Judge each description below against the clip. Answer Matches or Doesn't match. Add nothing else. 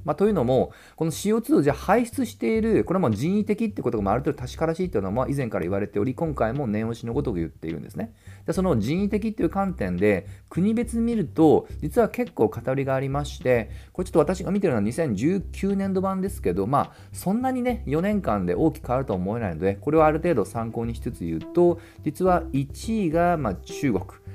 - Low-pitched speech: Doesn't match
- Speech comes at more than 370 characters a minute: Matches